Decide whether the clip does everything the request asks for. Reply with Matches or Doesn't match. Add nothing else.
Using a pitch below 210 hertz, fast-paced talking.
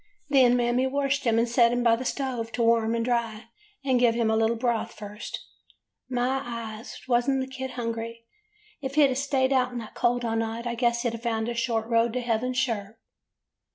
Doesn't match